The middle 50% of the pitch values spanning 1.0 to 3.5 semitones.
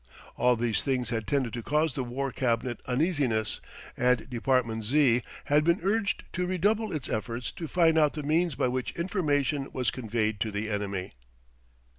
No: average, 5.1 semitones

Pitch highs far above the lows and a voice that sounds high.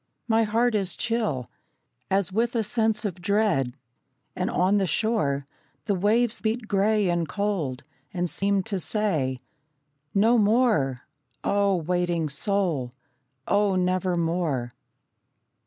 No: average, 4.2 semitones; high, 195 Hz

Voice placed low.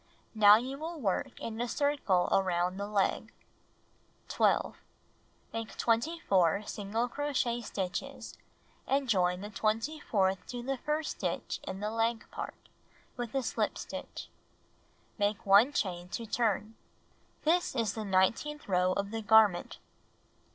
No: high, 220 Hz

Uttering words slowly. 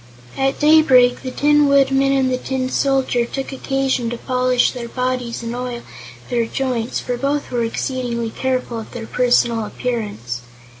No: average, 155 wpm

